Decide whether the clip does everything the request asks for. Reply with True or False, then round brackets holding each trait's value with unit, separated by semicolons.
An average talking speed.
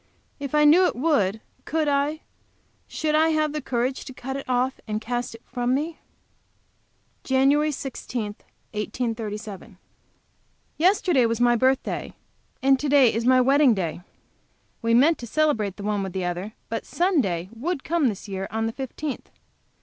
True (155 wpm)